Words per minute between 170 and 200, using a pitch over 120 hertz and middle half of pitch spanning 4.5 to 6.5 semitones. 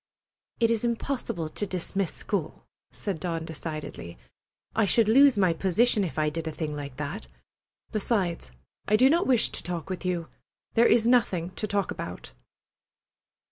No: average, 160 wpm; high, 190 Hz; wide, 5.6 semitones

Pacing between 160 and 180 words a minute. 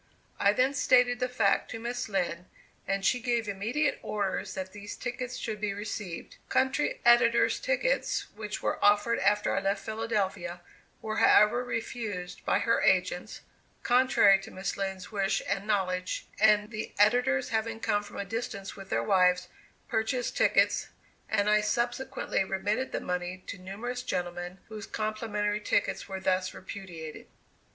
No: average, 150 wpm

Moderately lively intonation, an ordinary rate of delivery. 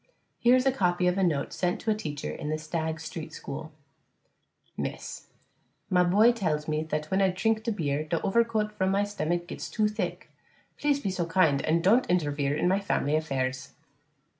Yes: average, 4.9 semitones; average, 190 wpm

